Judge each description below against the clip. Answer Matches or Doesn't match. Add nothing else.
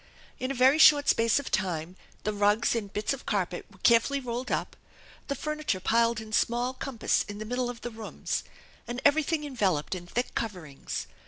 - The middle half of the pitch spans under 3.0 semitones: Doesn't match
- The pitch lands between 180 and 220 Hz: Doesn't match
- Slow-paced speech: Doesn't match